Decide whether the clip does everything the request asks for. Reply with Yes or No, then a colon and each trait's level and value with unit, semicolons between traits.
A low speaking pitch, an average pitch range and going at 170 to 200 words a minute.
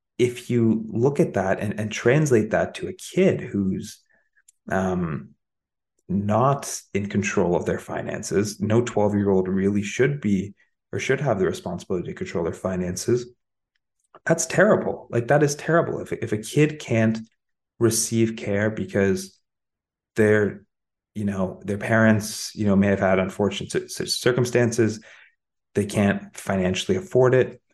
No: low, 105 Hz; average, 3.3 semitones; average, 145 wpm